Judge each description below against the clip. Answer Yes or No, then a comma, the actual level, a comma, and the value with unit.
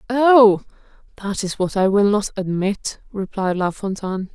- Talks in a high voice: Yes, high, 200 Hz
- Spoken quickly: No, average, 150 wpm